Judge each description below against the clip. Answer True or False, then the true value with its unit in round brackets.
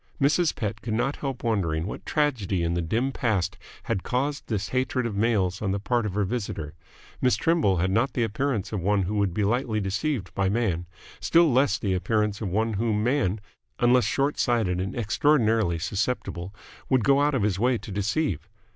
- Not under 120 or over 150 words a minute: False (195 wpm)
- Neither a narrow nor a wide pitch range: True (4.7 semitones)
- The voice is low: True (110 Hz)